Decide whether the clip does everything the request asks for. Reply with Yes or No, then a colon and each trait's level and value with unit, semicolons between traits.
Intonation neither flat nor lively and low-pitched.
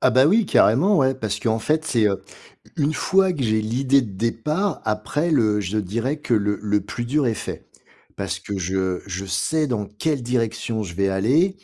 No: wide, 6.2 semitones; low, 115 Hz